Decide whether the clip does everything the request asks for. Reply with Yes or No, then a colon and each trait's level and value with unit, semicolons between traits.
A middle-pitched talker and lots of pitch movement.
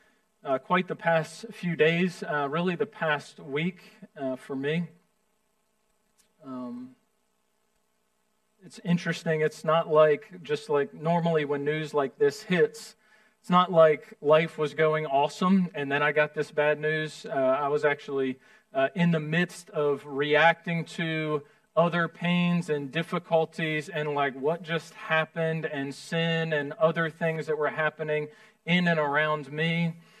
Yes: medium, 165 Hz; wide, 6.0 semitones